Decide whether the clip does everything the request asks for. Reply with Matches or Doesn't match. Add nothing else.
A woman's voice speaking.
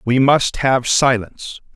Doesn't match